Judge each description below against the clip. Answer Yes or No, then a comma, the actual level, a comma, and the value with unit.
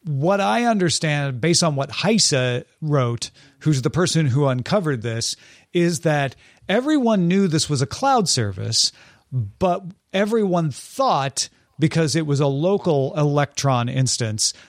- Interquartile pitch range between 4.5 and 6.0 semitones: Yes, average, 5.1 semitones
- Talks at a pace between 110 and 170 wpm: Yes, slow, 135 wpm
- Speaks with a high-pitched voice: No, medium, 155 Hz